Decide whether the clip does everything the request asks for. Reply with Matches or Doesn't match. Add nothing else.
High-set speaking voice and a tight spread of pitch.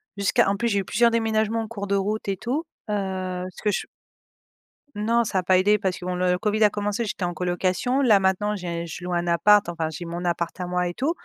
Doesn't match